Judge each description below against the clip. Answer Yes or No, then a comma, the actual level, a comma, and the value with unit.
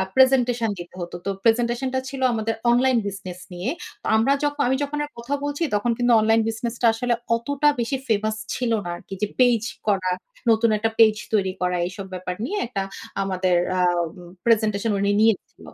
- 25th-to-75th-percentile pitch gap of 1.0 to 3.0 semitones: No, average, 3.9 semitones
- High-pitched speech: Yes, high, 225 Hz